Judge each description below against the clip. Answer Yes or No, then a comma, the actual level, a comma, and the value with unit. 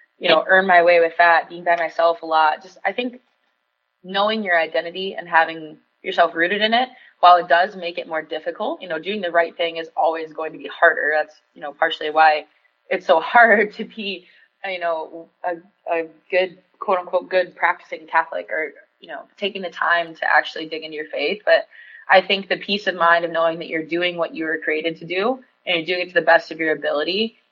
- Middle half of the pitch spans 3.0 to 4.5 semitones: No, narrow, 2.5 semitones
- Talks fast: Yes, fast, 220 wpm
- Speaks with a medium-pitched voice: Yes, medium, 170 Hz